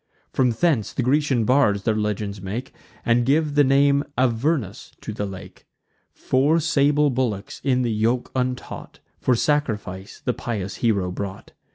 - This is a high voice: No, low, 125 Hz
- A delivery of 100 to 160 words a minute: Yes, average, 150 wpm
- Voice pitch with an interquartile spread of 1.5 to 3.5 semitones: No, average, 4.8 semitones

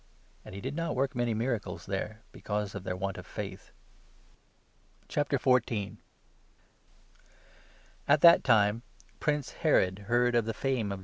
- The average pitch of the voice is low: Yes, low, 115 Hz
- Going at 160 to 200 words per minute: Yes, average, 165 wpm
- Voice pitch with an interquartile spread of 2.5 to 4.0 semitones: No, average, 4.5 semitones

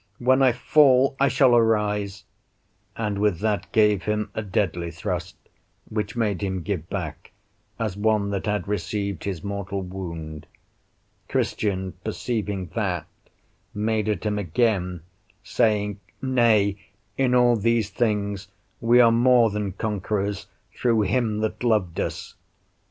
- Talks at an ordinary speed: No, slow, 130 wpm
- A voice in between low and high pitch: No, low, 105 Hz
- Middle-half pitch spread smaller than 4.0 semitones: Yes, average, 2.8 semitones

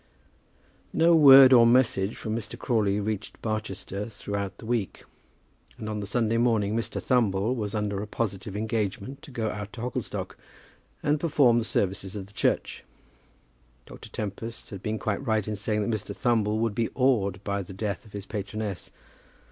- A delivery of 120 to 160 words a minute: No, average, 170 wpm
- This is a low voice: Yes, low, 110 Hz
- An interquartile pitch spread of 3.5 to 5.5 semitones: No, narrow, 2.5 semitones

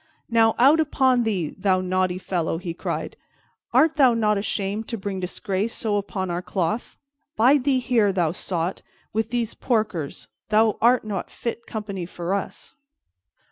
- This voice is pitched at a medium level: No, high, 210 Hz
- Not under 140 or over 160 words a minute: Yes, average, 155 wpm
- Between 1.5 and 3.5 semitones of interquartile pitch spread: No, average, 3.9 semitones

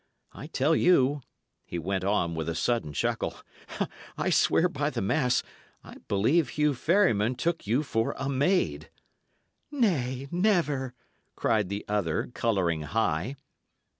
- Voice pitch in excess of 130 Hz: No, low, 125 Hz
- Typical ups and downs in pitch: No, wide, 7.2 semitones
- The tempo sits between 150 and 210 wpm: No, slow, 135 wpm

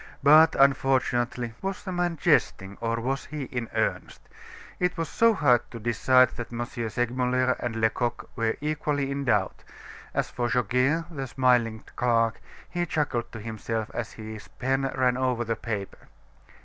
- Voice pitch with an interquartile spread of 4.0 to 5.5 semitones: No, average, 3.1 semitones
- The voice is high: No, low, 125 Hz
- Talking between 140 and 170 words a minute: Yes, average, 160 wpm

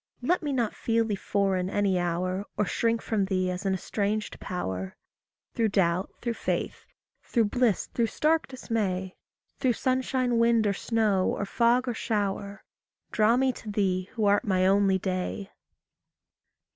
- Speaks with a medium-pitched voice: No, high, 205 Hz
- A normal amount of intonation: Yes, average, 3.5 semitones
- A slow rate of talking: No, average, 155 wpm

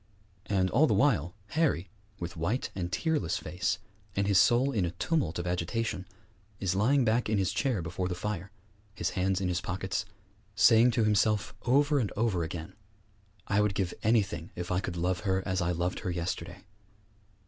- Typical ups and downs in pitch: Yes, average, 4.0 semitones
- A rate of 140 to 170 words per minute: No, average, 180 wpm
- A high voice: No, very low, 95 Hz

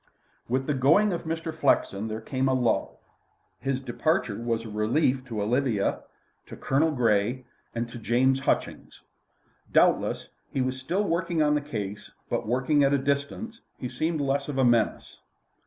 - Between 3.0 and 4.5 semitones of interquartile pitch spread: Yes, average, 3.9 semitones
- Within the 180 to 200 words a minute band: No, average, 165 wpm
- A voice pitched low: Yes, low, 130 Hz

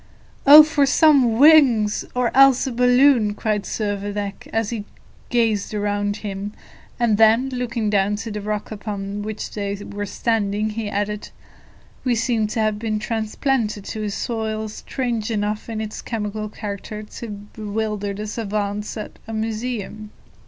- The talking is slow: No, average, 150 wpm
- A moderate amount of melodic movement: No, narrow, 2.0 semitones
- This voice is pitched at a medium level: No, high, 215 Hz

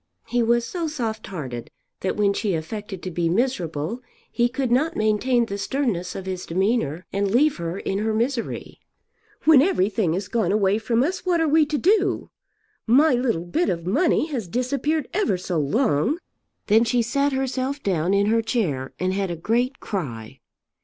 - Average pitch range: No, wide, 6.1 semitones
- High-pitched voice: Yes, high, 220 Hz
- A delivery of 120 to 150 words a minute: No, average, 180 wpm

